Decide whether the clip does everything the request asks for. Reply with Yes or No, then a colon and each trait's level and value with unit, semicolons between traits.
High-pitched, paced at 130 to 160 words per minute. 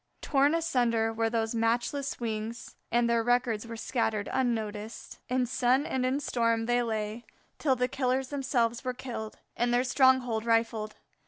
Yes: high, 240 Hz; average, 155 wpm